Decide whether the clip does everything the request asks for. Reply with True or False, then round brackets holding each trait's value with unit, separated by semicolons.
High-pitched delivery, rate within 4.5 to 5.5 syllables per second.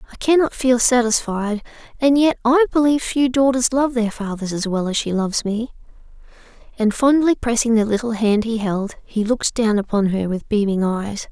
True (230 Hz; 5.2 syllables/s)